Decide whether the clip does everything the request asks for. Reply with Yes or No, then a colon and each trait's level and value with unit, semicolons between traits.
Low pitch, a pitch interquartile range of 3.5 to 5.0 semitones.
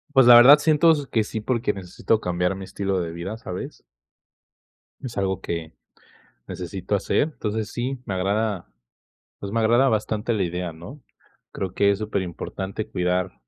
Yes: low, 100 Hz; average, 4.1 semitones